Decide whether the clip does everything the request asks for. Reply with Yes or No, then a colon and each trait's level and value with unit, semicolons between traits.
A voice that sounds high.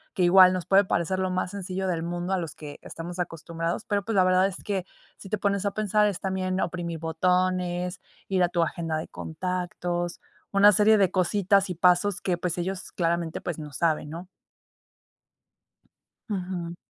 No: medium, 180 Hz